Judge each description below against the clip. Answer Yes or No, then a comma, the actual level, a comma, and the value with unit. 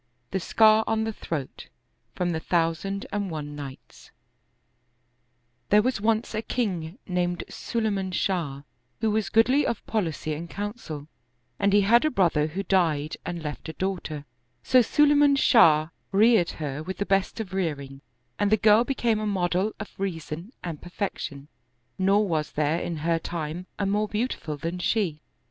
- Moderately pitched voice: Yes, medium, 180 Hz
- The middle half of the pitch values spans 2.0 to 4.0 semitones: No, average, 5.3 semitones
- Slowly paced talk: No, average, 160 wpm